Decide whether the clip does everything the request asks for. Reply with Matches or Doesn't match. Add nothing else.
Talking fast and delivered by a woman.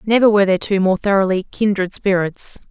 Doesn't match